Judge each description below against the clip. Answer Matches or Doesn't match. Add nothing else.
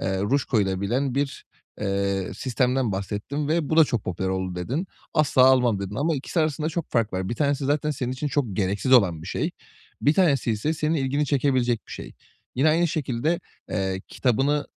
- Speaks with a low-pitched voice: Matches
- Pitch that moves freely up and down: Matches